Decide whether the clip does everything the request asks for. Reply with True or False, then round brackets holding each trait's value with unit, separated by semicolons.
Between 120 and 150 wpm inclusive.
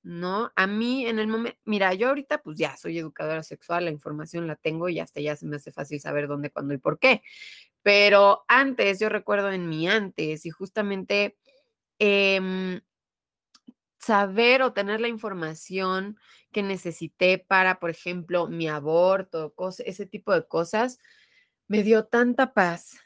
False (160 wpm)